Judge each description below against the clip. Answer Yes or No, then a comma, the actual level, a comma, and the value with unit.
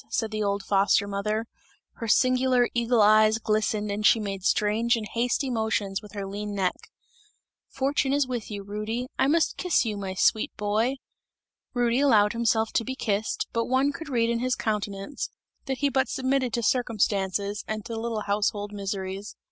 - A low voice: No, high, 220 Hz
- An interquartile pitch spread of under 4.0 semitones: Yes, average, 3.1 semitones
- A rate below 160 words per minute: No, average, 175 wpm